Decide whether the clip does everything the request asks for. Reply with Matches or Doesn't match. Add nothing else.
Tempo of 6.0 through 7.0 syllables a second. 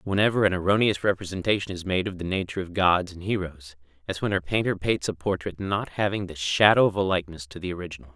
Matches